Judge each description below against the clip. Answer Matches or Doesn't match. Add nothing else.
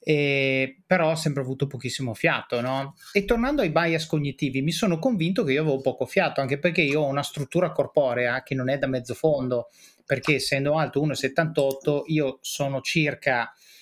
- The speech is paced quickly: Matches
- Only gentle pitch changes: Doesn't match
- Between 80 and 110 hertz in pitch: Doesn't match